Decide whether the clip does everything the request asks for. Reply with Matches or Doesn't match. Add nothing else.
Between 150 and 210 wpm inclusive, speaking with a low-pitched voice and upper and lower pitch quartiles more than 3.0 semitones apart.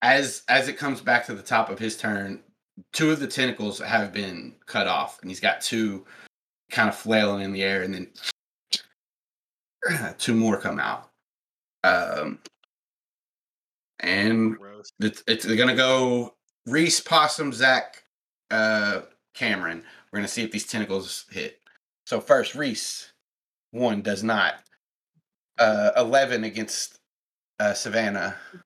Doesn't match